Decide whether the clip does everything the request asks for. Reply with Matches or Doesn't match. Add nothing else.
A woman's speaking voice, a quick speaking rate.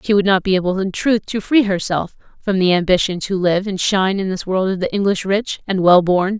Matches